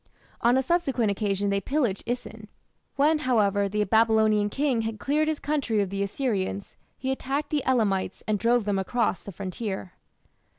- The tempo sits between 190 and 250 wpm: No, average, 165 wpm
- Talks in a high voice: Yes, high, 220 Hz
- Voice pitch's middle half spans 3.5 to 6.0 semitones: Yes, average, 4.6 semitones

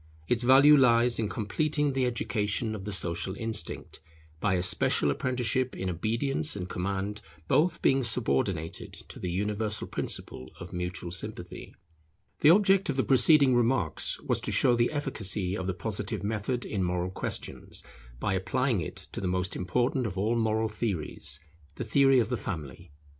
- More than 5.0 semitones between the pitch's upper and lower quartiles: Yes, wide, 5.5 semitones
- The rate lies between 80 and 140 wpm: No, average, 165 wpm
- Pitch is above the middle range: No, low, 110 Hz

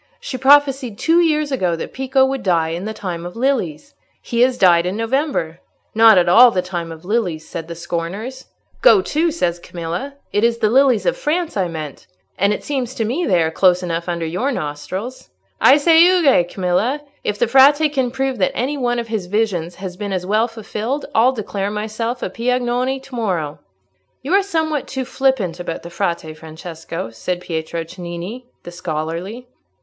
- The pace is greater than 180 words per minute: Yes, average, 190 wpm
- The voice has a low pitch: No, high, 215 Hz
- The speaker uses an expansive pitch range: Yes, wide, 7.3 semitones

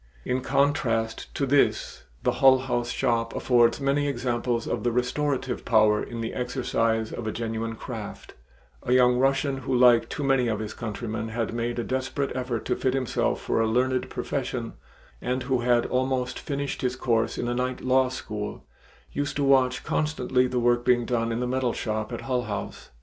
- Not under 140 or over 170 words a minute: No, average, 185 wpm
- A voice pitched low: Yes, low, 125 Hz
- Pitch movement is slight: Yes, narrow, 2.1 semitones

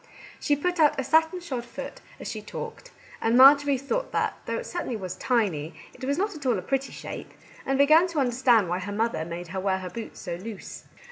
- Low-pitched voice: No, very high, 255 Hz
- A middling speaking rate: No, fast, 220 wpm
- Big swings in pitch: Yes, wide, 7.0 semitones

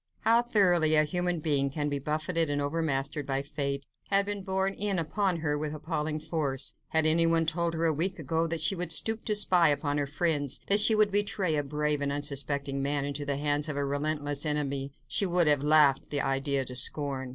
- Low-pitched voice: No, medium, 150 Hz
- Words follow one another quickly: Yes, fast, 210 wpm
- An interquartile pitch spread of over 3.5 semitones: No, average, 3.1 semitones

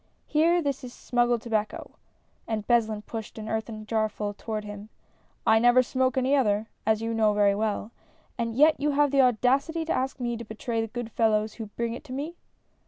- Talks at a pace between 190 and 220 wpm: Yes, average, 195 wpm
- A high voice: Yes, high, 230 Hz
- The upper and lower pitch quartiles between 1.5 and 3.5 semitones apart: Yes, average, 3.1 semitones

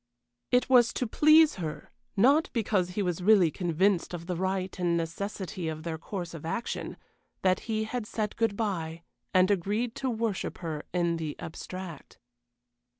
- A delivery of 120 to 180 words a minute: Yes, average, 160 wpm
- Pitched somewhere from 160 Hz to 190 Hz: Yes, medium, 185 Hz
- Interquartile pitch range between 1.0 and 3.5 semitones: No, average, 4.5 semitones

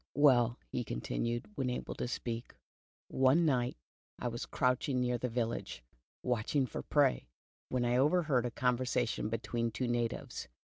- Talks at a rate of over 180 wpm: No, average, 145 wpm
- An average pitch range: No, narrow, 1.5 semitones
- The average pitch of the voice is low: Yes, low, 125 Hz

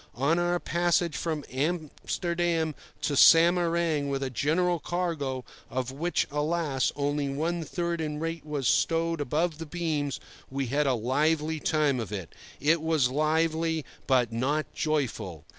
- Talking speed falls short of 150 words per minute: Yes, average, 140 wpm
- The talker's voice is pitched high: No, medium, 155 Hz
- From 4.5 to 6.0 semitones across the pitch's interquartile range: No, average, 3.2 semitones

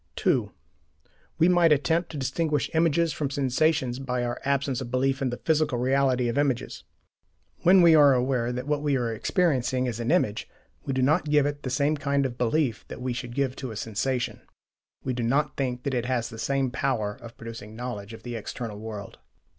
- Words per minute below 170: No, average, 200 wpm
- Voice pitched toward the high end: No, low, 130 Hz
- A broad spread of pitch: No, average, 3.2 semitones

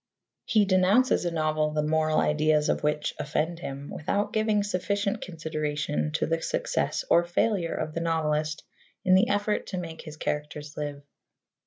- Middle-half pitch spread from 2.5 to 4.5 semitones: Yes, average, 3.6 semitones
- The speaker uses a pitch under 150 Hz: No, medium, 160 Hz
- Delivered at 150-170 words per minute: Yes, average, 160 wpm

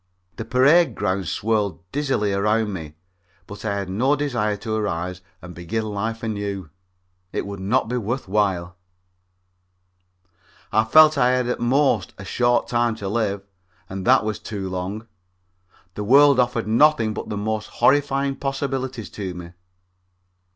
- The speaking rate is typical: Yes, average, 160 wpm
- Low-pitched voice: Yes, low, 110 Hz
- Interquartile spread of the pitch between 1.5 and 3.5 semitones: No, average, 4.3 semitones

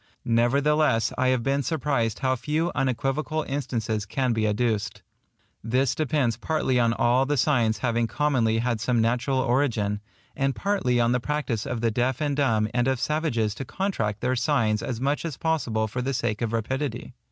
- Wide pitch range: No, average, 3.5 semitones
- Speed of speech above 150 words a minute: Yes, average, 175 wpm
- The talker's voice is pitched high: No, low, 125 Hz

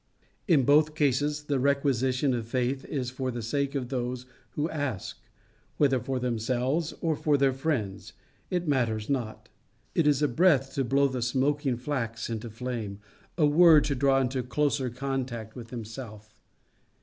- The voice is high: No, low, 130 Hz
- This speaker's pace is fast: No, average, 160 wpm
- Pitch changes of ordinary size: Yes, average, 3.1 semitones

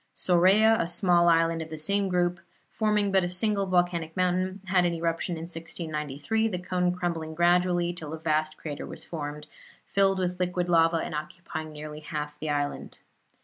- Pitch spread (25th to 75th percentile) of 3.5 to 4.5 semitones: No, narrow, 2.5 semitones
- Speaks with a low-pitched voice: No, medium, 175 Hz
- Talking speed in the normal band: Yes, average, 175 wpm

